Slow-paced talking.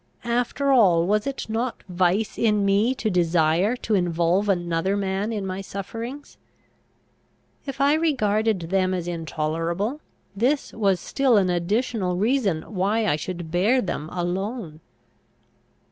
Yes: slow, 130 wpm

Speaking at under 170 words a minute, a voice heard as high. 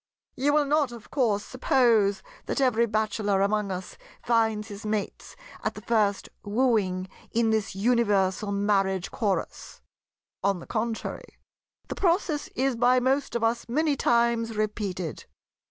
Yes: average, 140 wpm; high, 220 Hz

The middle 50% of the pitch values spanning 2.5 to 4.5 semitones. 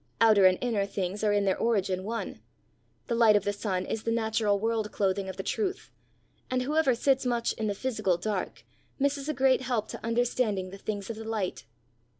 Yes: average, 3.3 semitones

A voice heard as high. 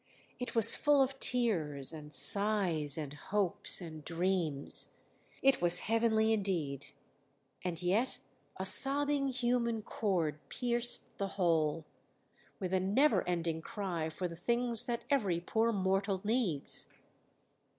Yes: high, 195 Hz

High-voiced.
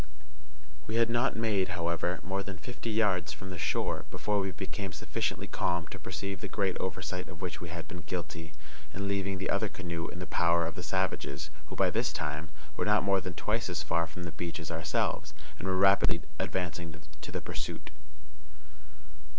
No: very low, 90 Hz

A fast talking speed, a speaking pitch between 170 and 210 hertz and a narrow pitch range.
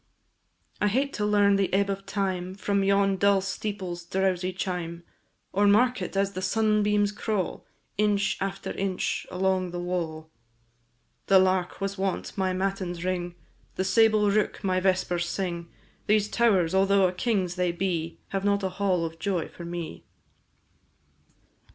No: average, 150 wpm; high, 190 Hz; narrow, 2.0 semitones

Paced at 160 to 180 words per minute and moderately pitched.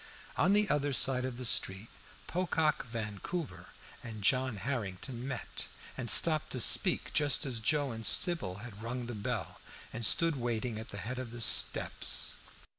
No: average, 165 wpm; low, 125 Hz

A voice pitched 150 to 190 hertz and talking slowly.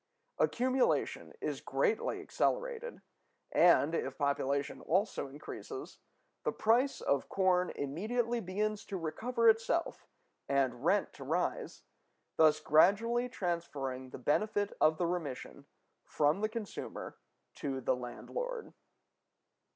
Yes: medium, 185 Hz; slow, 110 wpm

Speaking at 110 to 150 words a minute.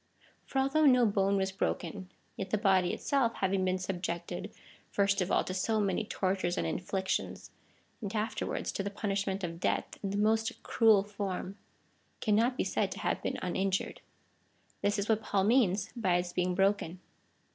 No: average, 175 wpm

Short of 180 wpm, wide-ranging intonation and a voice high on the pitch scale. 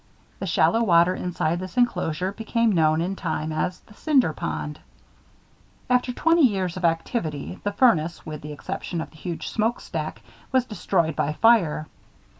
No: average, 160 wpm; wide, 6.3 semitones; medium, 180 Hz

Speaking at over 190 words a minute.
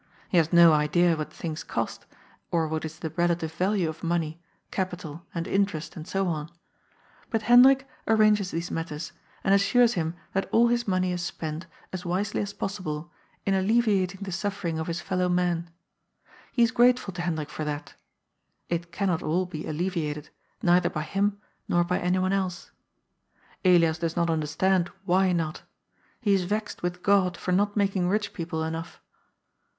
No: average, 170 wpm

